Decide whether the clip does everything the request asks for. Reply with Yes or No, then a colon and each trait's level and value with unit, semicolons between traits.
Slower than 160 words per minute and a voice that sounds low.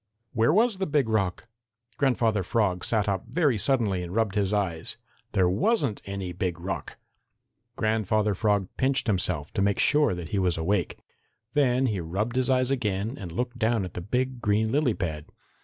No: average, 175 wpm; low, 105 Hz